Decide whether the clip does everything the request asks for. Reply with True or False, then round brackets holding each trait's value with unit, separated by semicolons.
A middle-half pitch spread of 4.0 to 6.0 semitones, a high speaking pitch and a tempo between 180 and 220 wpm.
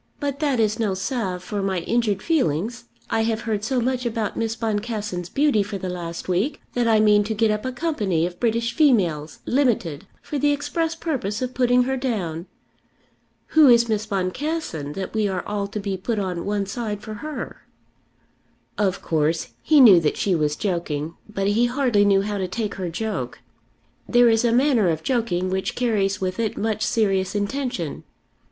True (4.3 semitones; 215 Hz; 185 wpm)